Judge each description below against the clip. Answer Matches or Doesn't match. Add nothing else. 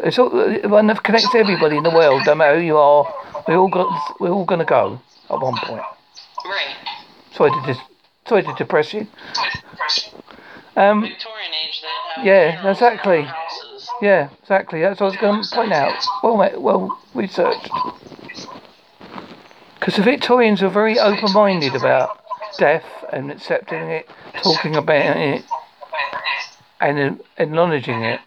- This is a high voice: Matches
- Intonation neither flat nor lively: Doesn't match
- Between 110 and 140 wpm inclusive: Matches